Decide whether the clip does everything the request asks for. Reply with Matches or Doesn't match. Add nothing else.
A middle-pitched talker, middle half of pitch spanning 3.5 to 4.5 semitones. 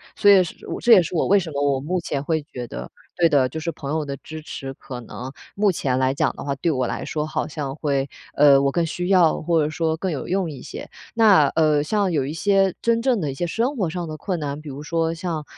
Matches